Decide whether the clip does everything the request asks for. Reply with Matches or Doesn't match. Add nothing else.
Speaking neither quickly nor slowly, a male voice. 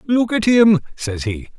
Matches